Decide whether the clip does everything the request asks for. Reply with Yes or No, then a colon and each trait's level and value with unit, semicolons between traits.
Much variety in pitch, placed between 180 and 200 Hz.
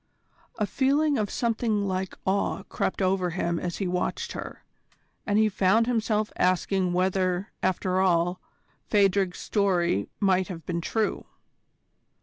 No: narrow, 2.6 semitones; high, 190 Hz